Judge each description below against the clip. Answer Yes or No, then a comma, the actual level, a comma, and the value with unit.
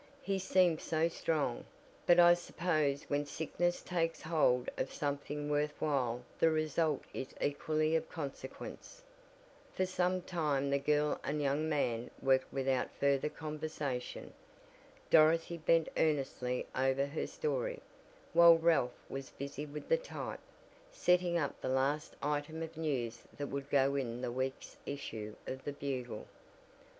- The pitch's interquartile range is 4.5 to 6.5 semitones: No, average, 3.2 semitones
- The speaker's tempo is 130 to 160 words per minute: Yes, average, 140 wpm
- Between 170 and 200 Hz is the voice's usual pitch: No, medium, 150 Hz